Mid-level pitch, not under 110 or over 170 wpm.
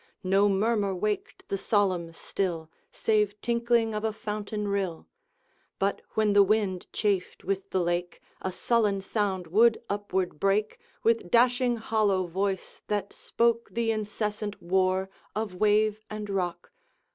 No: high, 205 Hz; slow, 135 wpm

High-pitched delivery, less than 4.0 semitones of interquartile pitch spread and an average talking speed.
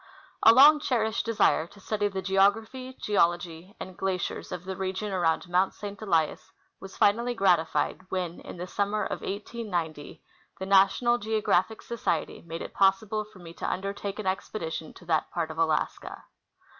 Yes: high, 195 Hz; average, 3.4 semitones; average, 160 wpm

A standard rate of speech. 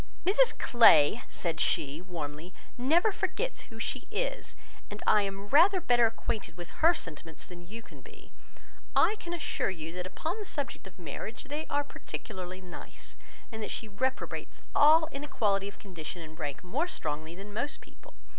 Yes: average, 175 wpm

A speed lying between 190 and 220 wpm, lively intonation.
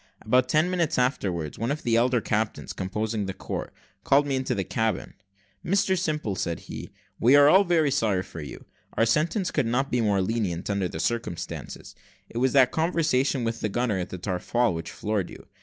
Yes: average, 195 wpm; wide, 6.0 semitones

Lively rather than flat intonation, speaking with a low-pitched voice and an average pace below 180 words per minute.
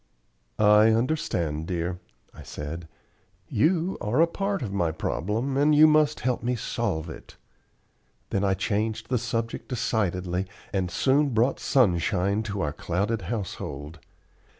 Yes: wide, 6.1 semitones; low, 105 Hz; slow, 135 wpm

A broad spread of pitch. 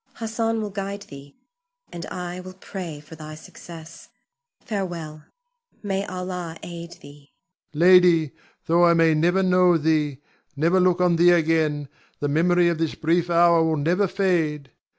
No: narrow, 2.5 semitones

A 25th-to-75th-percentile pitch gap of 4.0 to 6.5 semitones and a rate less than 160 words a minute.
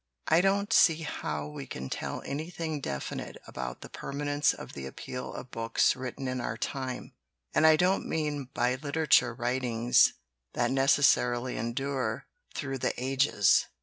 No: average, 3.6 semitones; average, 150 wpm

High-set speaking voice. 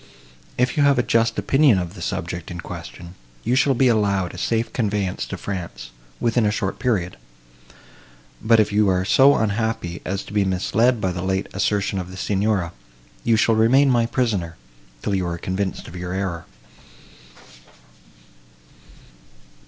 No: low, 100 Hz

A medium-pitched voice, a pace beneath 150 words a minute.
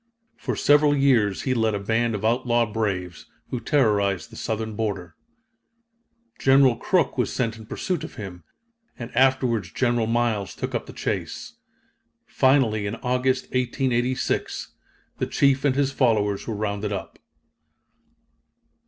No: low, 115 Hz; slow, 135 wpm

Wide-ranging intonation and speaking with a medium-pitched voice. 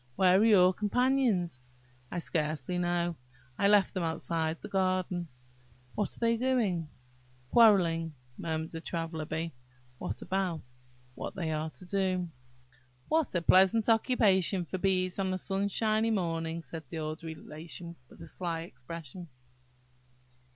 No: average, 3.1 semitones; medium, 175 Hz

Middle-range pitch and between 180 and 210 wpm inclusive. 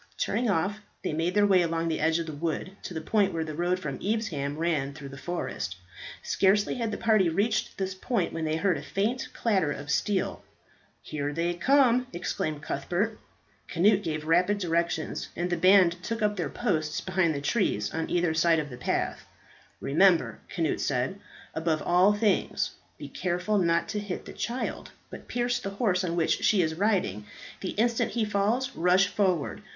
Yes: medium, 180 Hz; average, 185 wpm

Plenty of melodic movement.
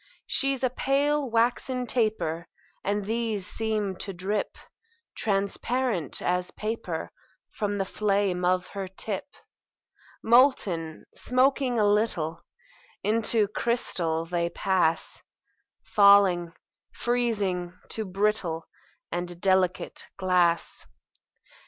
No: average, 4.3 semitones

